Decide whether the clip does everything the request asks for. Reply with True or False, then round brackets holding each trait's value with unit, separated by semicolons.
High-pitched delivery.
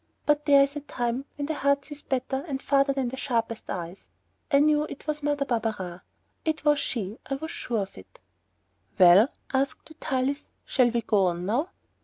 True (270 Hz)